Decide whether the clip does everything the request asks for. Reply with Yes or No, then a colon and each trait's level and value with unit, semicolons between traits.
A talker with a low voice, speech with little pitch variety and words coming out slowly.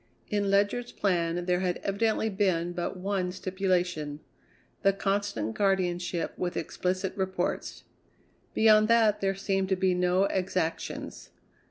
No: high, 190 Hz; narrow, 1.9 semitones; slow, 125 wpm